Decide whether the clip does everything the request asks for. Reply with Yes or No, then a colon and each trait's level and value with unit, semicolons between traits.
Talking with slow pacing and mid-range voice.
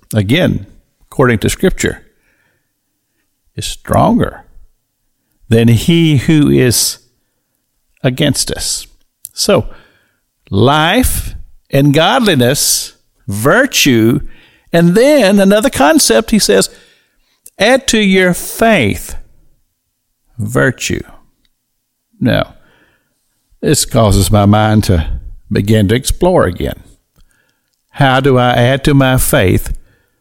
No: slow, 90 wpm; low, 130 Hz